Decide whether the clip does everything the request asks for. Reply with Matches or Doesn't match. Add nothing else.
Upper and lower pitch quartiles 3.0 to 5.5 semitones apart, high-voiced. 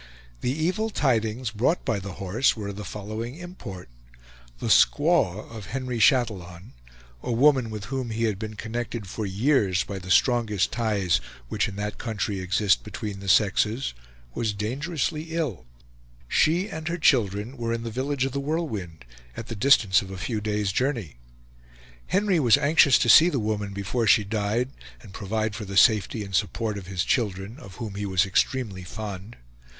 Doesn't match